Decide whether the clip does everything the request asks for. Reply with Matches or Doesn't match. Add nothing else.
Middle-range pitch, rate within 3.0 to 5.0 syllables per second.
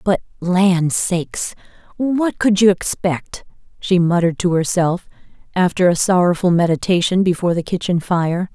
Matches